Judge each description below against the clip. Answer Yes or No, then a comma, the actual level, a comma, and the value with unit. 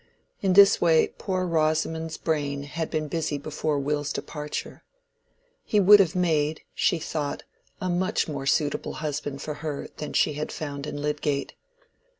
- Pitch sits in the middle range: Yes, medium, 155 Hz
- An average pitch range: No, narrow, 2.2 semitones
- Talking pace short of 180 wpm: Yes, average, 155 wpm